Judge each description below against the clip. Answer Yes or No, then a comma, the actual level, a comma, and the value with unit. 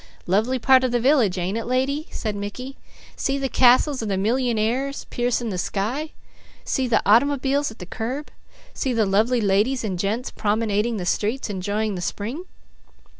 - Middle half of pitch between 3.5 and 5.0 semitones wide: Yes, average, 4.1 semitones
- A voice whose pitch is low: No, high, 230 Hz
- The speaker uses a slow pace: No, average, 170 wpm